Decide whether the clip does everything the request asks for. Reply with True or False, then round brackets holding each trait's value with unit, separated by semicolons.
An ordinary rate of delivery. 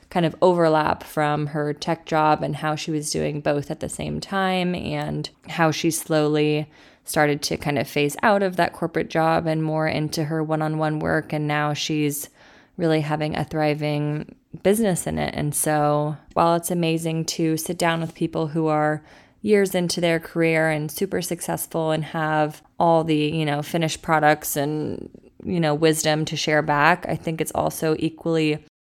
True (180 wpm)